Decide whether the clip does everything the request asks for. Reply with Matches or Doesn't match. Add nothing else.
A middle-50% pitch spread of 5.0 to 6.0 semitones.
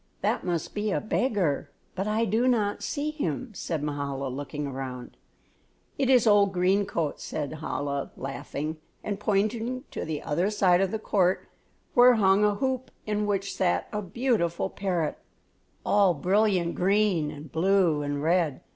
Matches